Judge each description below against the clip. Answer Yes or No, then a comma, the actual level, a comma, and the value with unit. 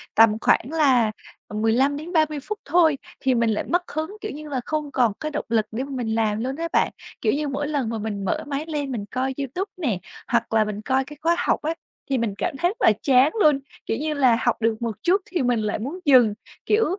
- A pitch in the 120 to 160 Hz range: No, very high, 270 Hz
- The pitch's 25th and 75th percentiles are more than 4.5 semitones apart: Yes, average, 5.2 semitones